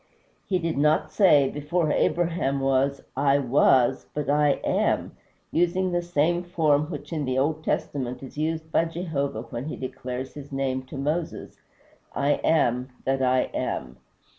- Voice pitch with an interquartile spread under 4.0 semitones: Yes, average, 3.5 semitones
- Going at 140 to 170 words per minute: Yes, average, 155 wpm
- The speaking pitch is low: No, medium, 145 Hz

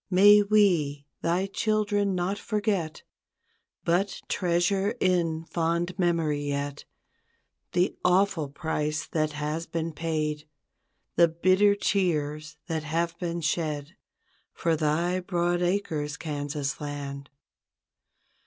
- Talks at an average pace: No, slow, 105 wpm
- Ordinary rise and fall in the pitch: Yes, average, 3.5 semitones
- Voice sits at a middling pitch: Yes, medium, 170 Hz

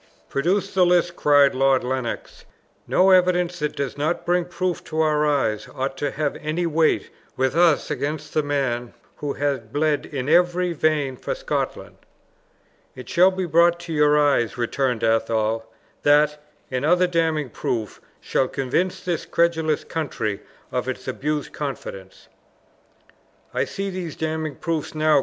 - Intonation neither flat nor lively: Yes, average, 4.0 semitones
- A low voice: No, medium, 150 Hz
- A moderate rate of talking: Yes, average, 150 wpm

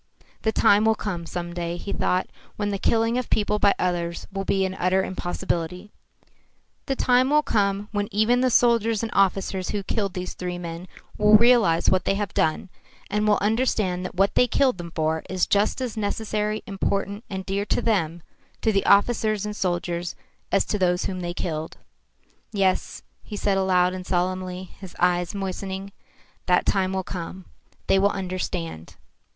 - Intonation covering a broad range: No, average, 2.7 semitones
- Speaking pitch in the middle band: No, high, 195 Hz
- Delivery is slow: No, average, 175 wpm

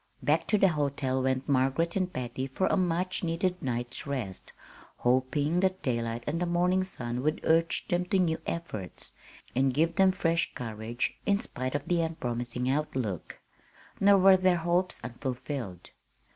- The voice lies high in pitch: No, medium, 145 Hz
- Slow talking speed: No, average, 160 wpm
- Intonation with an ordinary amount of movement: No, wide, 6.0 semitones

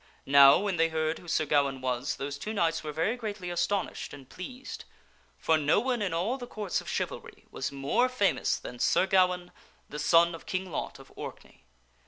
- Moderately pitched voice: Yes, medium, 170 Hz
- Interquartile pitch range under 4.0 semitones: No, wide, 5.4 semitones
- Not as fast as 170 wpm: No, average, 200 wpm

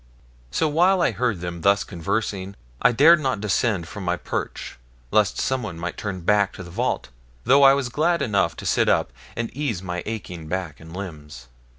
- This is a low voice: Yes, low, 100 Hz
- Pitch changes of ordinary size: No, wide, 6.1 semitones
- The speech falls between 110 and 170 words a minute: No, average, 190 wpm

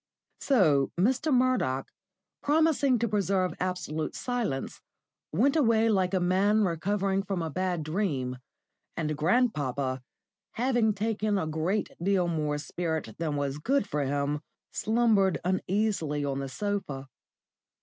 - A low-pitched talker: No, medium, 185 Hz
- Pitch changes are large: Yes, wide, 6.3 semitones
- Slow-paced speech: Yes, slow, 125 wpm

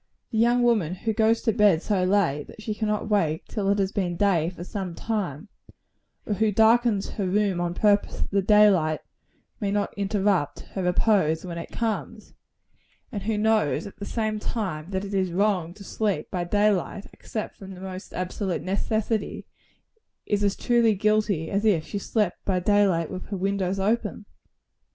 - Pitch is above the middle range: Yes, high, 200 Hz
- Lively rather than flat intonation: No, narrow, 2.6 semitones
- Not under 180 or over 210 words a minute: Yes, average, 185 wpm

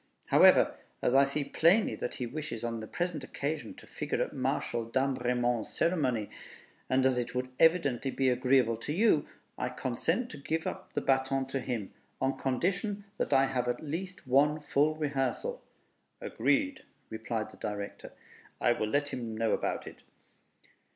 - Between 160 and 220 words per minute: Yes, average, 165 wpm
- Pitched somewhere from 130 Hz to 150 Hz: Yes, low, 135 Hz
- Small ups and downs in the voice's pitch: No, average, 4.2 semitones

